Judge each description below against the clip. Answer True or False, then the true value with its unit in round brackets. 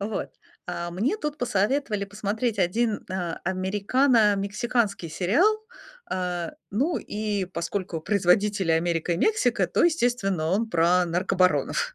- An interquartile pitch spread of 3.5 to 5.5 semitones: True (4.7 semitones)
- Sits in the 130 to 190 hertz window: False (200 Hz)